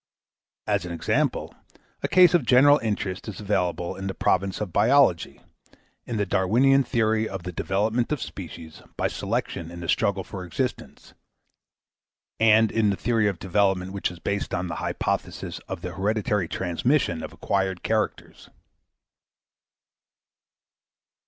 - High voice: No, low, 100 Hz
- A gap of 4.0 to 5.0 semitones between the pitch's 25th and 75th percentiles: No, average, 3.4 semitones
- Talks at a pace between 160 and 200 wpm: No, average, 140 wpm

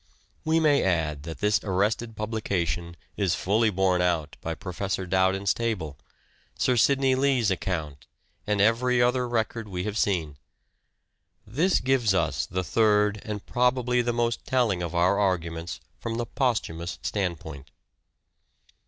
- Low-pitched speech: Yes, low, 105 Hz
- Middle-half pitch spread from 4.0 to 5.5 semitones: Yes, average, 4.9 semitones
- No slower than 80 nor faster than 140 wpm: Yes, slow, 135 wpm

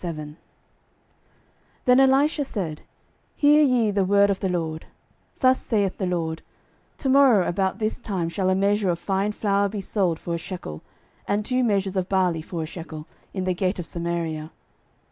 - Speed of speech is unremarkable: Yes, average, 175 wpm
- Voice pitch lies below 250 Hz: Yes, high, 190 Hz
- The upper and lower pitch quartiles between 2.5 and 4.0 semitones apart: Yes, average, 3.7 semitones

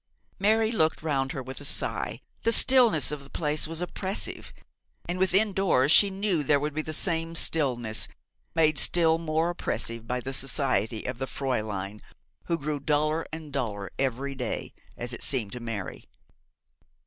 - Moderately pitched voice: Yes, medium, 150 Hz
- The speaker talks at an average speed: Yes, average, 165 wpm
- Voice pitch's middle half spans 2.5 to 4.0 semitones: No, average, 4.5 semitones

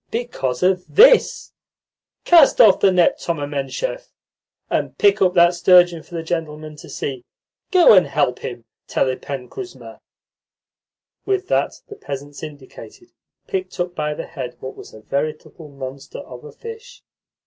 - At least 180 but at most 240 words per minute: No, average, 150 wpm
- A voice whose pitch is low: No, medium, 165 Hz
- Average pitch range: No, wide, 8.6 semitones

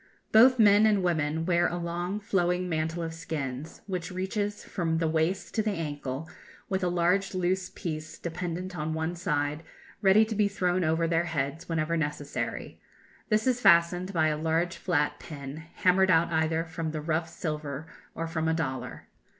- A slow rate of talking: No, average, 175 wpm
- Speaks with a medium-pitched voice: Yes, medium, 170 Hz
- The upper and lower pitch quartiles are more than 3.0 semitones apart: No, narrow, 2.6 semitones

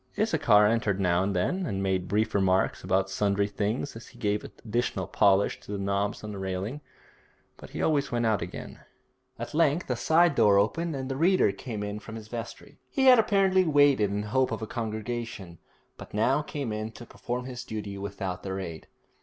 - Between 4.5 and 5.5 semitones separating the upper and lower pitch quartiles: Yes, average, 4.9 semitones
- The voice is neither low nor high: No, low, 110 Hz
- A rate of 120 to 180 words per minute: No, average, 195 wpm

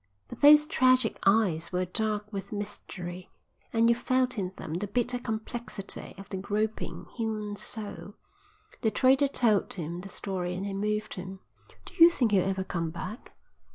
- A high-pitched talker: Yes, high, 210 Hz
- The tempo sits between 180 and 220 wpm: No, average, 165 wpm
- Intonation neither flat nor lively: Yes, average, 3.4 semitones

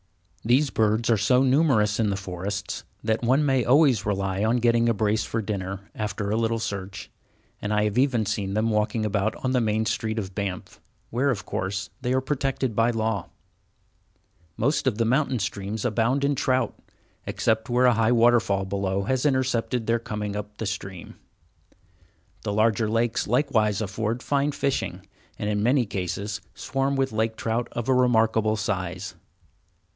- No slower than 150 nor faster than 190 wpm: Yes, average, 170 wpm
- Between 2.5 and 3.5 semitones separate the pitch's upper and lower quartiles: Yes, average, 3.1 semitones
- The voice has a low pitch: Yes, low, 110 Hz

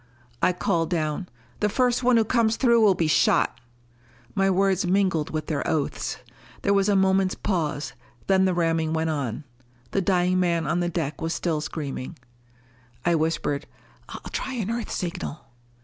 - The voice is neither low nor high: Yes, medium, 180 Hz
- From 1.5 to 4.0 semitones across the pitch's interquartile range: Yes, average, 3.6 semitones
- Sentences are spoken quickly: No, average, 165 wpm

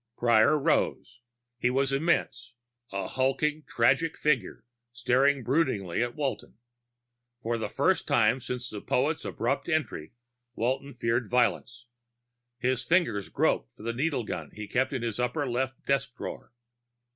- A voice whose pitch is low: Yes, low, 125 Hz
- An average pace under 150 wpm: Yes, average, 140 wpm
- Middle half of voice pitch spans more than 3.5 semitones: No, average, 2.9 semitones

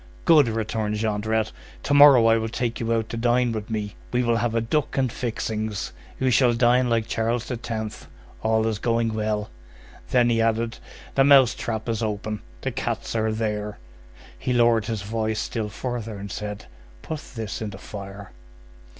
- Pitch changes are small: Yes, narrow, 1.7 semitones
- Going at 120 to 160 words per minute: No, average, 180 wpm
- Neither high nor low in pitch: No, low, 115 Hz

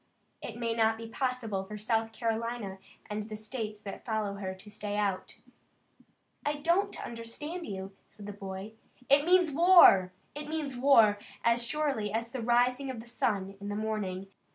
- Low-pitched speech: No, high, 225 Hz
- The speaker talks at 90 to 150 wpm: No, average, 170 wpm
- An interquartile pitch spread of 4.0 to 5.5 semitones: No, average, 3.6 semitones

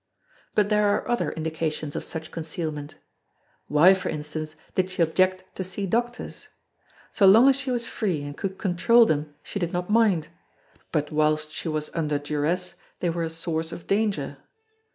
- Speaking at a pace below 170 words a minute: No, average, 175 wpm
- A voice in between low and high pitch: Yes, medium, 170 Hz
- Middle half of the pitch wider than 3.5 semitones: Yes, average, 4.3 semitones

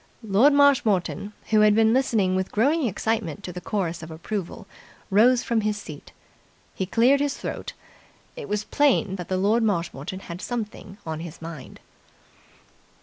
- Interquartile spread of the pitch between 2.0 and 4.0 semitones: No, average, 4.4 semitones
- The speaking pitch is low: No, high, 210 Hz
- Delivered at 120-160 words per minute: Yes, average, 150 wpm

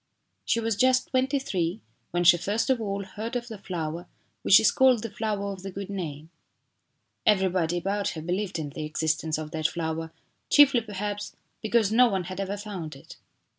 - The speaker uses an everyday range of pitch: Yes, average, 4.4 semitones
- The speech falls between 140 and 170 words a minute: No, average, 185 wpm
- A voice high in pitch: Yes, high, 195 Hz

